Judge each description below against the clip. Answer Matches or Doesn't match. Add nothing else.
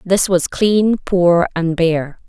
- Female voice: Matches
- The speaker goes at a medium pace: Matches